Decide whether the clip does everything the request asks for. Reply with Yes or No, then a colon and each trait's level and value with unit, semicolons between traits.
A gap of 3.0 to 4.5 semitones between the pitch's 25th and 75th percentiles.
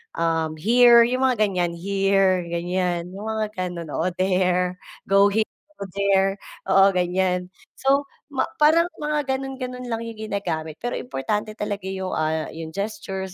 Yes: average, 3.8 semitones